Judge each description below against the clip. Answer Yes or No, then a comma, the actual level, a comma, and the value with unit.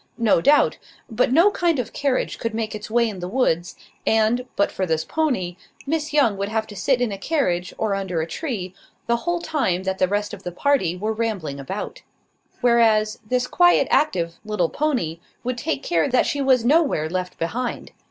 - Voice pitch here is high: Yes, high, 220 Hz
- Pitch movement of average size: No, wide, 6.0 semitones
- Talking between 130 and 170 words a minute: No, average, 195 wpm